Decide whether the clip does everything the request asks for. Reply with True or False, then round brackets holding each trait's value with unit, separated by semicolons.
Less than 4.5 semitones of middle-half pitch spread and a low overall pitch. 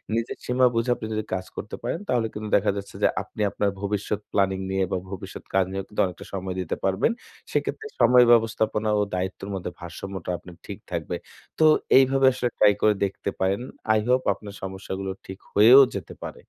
True (3.2 semitones; 100 Hz)